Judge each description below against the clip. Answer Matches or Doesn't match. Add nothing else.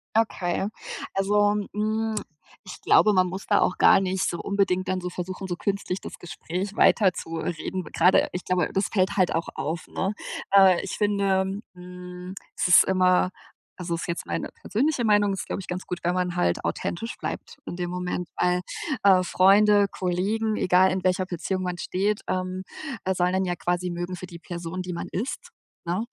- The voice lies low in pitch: Doesn't match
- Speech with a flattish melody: Matches